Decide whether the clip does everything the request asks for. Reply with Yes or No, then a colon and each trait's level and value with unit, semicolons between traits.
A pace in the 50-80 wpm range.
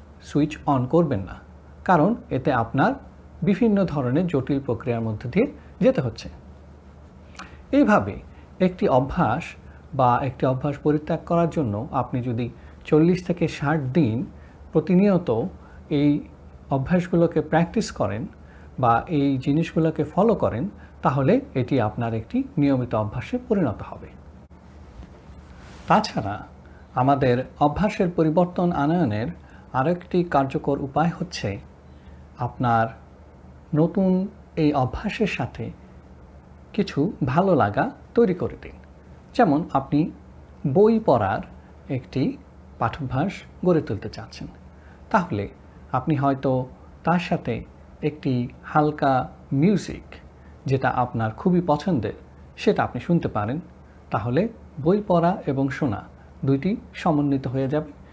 No: average, 105 wpm